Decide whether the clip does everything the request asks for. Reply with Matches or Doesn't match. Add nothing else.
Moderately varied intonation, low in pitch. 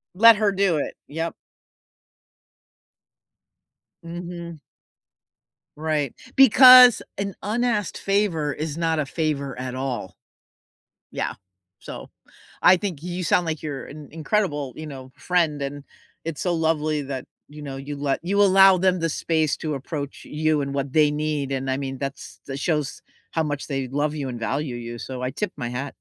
Doesn't match